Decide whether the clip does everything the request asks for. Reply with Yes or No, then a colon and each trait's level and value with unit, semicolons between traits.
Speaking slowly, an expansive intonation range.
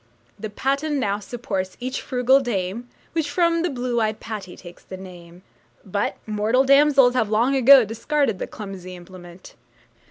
No: average, 155 wpm; wide, 5.8 semitones